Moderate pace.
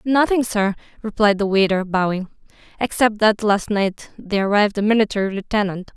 Yes: average, 150 wpm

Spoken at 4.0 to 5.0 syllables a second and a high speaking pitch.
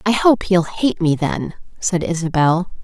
No: 4.3 syllables/s; medium, 180 Hz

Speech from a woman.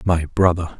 No: male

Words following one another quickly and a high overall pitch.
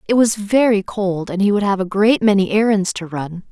Yes: fast, 240 wpm; high, 200 Hz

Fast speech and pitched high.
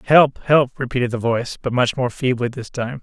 No: fast, 220 wpm; low, 125 Hz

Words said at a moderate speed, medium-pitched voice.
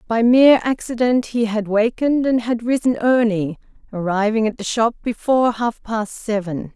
No: average, 160 wpm; high, 230 Hz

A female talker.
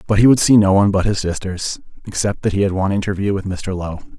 No: male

